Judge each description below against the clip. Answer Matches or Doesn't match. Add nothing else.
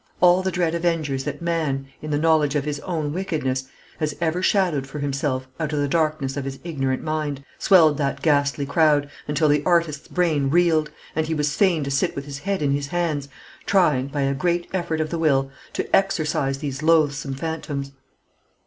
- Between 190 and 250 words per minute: Matches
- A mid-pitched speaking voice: Matches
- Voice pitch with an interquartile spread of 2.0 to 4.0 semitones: Matches